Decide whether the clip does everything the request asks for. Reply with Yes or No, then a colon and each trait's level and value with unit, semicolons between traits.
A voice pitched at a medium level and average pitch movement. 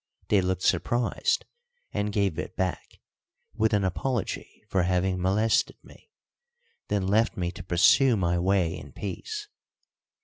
No: very low, 95 Hz; average, 3.1 semitones